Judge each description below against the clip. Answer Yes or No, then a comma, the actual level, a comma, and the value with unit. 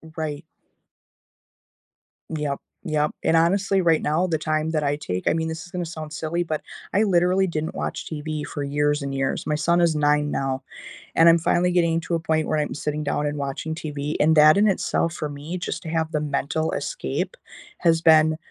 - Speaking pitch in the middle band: Yes, medium, 155 Hz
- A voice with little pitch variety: Yes, narrow, 2.1 semitones